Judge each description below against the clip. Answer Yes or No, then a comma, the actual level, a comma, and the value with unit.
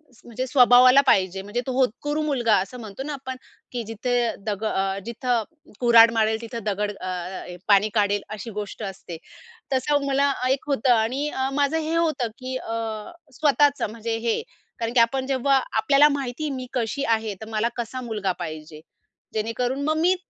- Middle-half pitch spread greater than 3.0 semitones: Yes, average, 3.8 semitones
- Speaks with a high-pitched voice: Yes, high, 235 Hz